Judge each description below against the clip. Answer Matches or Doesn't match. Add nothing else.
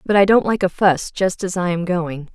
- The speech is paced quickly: Matches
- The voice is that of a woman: Matches